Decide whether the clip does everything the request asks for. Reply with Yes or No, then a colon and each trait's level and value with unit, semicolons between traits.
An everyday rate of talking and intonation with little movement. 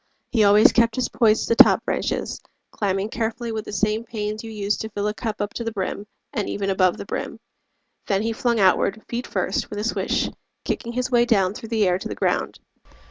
No: fast, 225 wpm; narrow, 2.2 semitones